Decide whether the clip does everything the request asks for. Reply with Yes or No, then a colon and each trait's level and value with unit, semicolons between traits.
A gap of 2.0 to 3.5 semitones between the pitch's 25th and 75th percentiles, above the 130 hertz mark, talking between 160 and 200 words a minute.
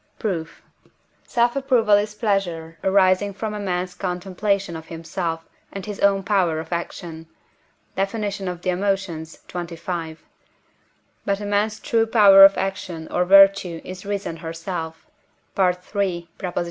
No: average, 3.0 semitones; high, 190 Hz; slow, 135 wpm